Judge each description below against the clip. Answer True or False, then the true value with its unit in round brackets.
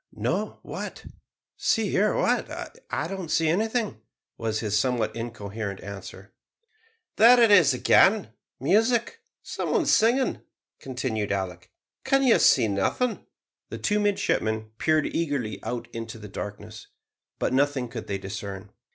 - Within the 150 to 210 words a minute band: False (135 wpm)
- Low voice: True (120 Hz)